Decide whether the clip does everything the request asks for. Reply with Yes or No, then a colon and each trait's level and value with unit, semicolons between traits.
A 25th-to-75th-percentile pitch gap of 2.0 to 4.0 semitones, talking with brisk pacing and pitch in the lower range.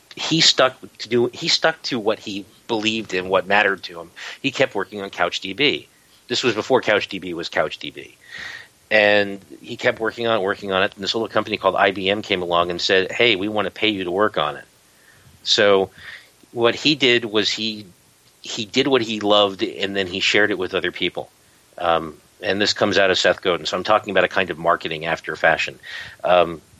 Yes: average, 2.9 semitones; fast, 210 wpm; low, 105 Hz